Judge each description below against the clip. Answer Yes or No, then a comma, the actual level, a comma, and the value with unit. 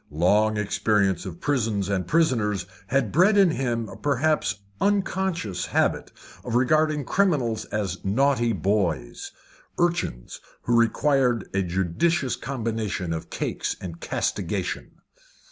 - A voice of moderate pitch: No, low, 115 Hz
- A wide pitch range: Yes, wide, 6.9 semitones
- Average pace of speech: No, slow, 115 wpm